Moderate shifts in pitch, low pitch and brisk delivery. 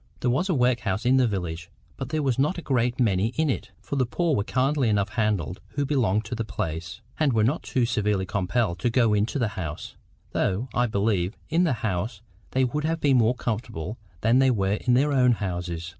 Yes: average, 4.7 semitones; low, 115 Hz; fast, 220 wpm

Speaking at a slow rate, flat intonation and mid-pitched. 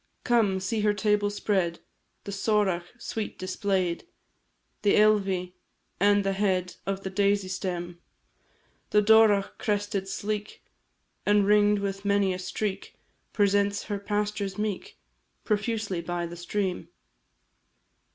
No: slow, 120 wpm; narrow, 1.7 semitones; high, 200 Hz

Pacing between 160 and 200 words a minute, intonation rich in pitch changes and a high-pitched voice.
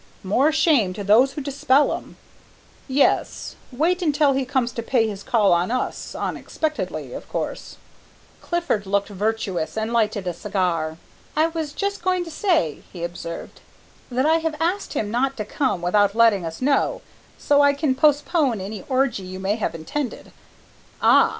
Yes: average, 170 wpm; wide, 6.8 semitones; high, 245 Hz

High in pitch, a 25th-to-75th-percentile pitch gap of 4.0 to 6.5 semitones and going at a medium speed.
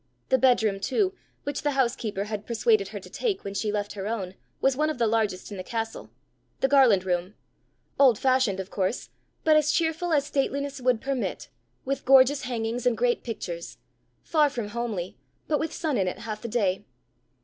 Yes: high, 240 Hz; average, 5.0 semitones; average, 190 wpm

